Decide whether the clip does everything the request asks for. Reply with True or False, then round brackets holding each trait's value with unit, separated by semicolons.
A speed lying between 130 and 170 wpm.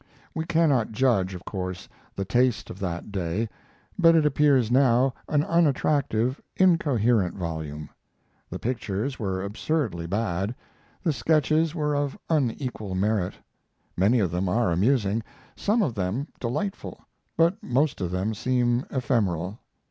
True (135 wpm)